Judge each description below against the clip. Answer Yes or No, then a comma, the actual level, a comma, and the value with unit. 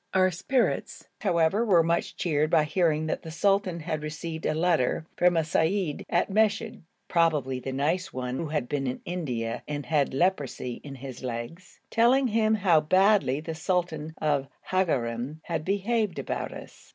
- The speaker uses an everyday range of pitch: Yes, average, 4.3 semitones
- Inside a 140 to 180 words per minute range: Yes, average, 170 wpm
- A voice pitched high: No, medium, 160 Hz